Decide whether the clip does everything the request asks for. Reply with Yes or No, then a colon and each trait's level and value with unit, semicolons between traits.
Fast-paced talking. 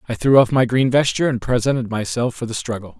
Yes: fast, 240 wpm